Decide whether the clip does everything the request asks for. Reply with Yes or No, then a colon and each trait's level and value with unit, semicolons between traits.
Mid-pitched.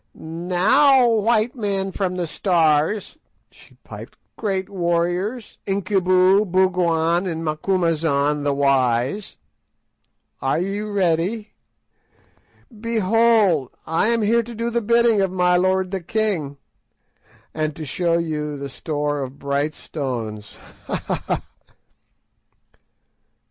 Yes: medium, 180 Hz